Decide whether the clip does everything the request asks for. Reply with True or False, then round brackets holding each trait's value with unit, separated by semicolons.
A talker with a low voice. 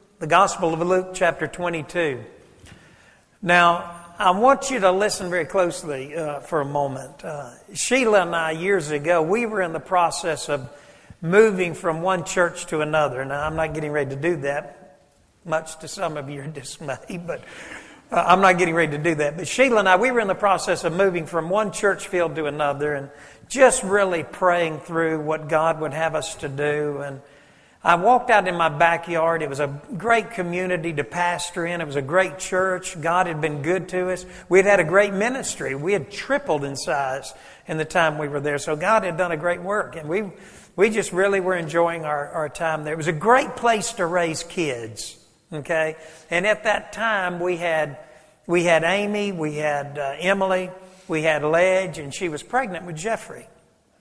False (170 Hz)